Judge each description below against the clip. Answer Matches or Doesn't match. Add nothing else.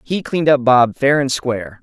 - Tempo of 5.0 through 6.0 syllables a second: Matches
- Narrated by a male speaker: Matches